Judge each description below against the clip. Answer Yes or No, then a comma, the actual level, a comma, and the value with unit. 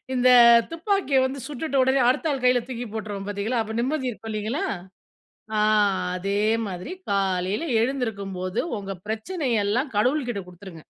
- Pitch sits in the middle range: No, high, 225 Hz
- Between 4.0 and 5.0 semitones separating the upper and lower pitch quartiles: Yes, average, 4.7 semitones